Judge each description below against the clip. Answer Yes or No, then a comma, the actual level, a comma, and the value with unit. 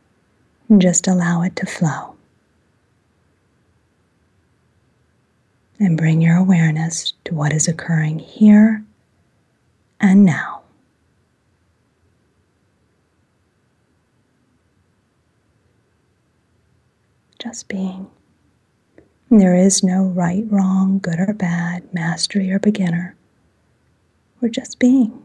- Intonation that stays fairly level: No, average, 3.7 semitones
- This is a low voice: No, medium, 180 Hz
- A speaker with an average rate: No, slow, 80 wpm